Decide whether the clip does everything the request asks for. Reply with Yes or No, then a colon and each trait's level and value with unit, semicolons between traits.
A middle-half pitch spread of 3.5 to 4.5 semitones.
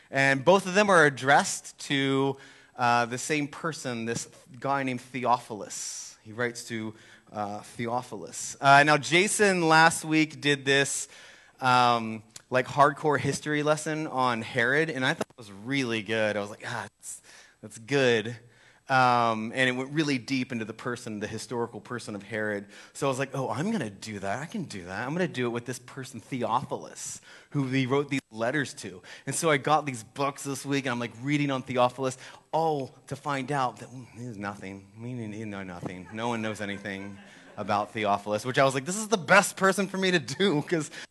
Yes: average, 4.2 semitones